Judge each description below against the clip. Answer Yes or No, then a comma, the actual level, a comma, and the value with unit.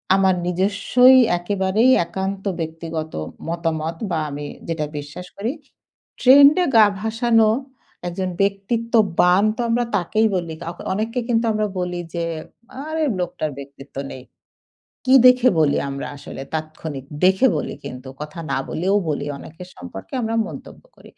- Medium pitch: Yes, medium, 180 Hz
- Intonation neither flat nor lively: No, wide, 5.8 semitones